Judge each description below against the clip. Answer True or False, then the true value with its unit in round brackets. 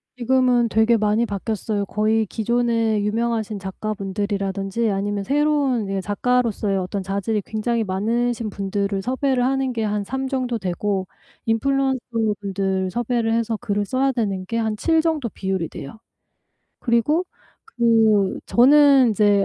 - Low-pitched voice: False (220 Hz)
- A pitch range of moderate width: True (3.3 semitones)